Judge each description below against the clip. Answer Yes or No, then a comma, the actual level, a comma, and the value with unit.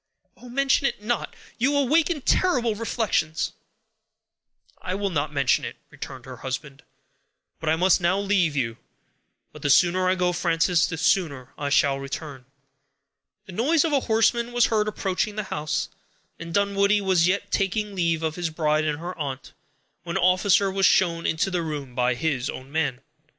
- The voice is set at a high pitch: No, medium, 180 Hz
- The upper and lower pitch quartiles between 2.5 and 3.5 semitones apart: No, average, 5.3 semitones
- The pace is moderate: Yes, average, 170 wpm